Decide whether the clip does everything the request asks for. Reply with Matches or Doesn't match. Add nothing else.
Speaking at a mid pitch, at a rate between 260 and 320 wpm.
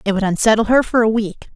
Doesn't match